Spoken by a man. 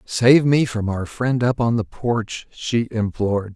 Yes: male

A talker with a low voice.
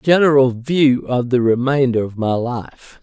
Yes: low, 130 Hz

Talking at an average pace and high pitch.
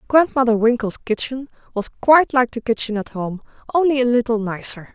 Yes: average, 170 wpm; high, 240 Hz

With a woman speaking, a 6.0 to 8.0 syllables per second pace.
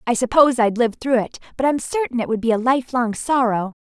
Yes: female; 6.1 syllables/s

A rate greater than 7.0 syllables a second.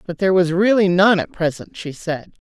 No: 5.4 syllables/s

